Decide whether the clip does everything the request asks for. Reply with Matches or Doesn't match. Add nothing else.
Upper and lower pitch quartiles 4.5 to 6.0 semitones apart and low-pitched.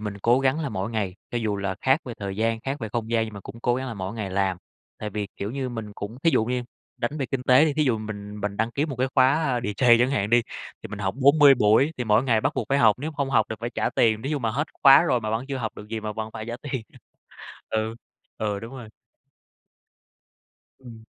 Doesn't match